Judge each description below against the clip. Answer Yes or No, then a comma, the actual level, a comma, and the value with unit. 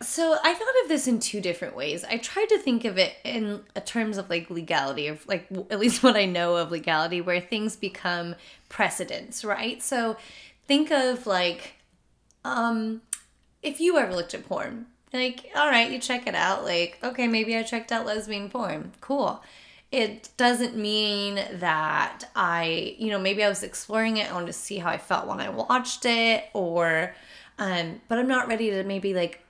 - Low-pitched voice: No, high, 220 Hz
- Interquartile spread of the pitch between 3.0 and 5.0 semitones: No, wide, 5.4 semitones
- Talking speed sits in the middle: Yes, average, 190 wpm